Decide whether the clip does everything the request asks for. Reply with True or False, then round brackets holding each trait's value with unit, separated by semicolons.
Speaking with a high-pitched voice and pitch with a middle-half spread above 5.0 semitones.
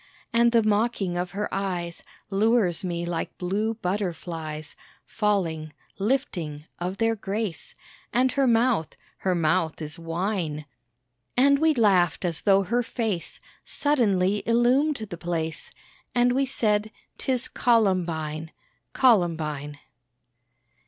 True (195 Hz; 5.4 semitones)